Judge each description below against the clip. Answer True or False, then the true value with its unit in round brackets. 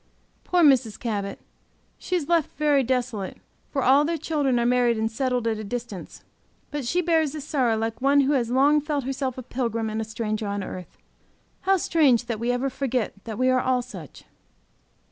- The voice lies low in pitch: False (255 Hz)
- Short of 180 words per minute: False (195 wpm)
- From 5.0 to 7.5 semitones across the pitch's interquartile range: False (3.9 semitones)